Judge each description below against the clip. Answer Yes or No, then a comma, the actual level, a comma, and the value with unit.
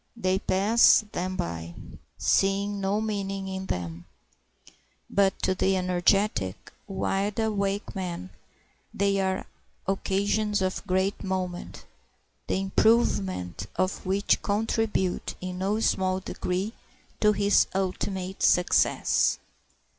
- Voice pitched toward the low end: No, high, 190 Hz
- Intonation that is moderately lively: No, narrow, 1.6 semitones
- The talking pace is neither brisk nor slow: No, slow, 105 wpm